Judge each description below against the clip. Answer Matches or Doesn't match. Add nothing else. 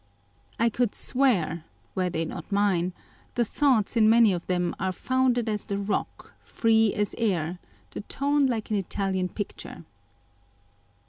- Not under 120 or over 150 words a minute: Matches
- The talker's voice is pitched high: Matches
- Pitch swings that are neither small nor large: Matches